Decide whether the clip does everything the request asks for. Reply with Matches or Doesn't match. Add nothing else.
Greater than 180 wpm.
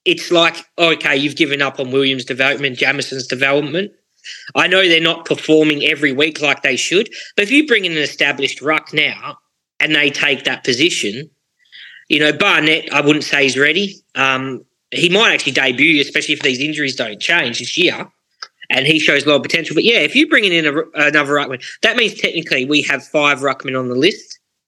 Matches